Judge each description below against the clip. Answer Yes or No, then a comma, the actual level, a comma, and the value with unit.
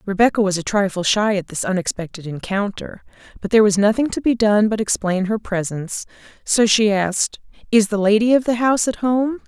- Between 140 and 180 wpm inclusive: No, average, 195 wpm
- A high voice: Yes, high, 210 Hz